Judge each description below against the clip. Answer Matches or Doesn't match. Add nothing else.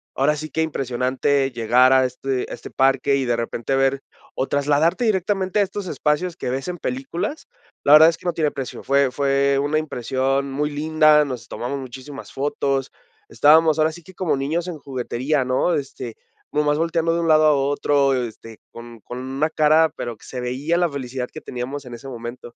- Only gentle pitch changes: Doesn't match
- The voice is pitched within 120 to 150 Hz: Matches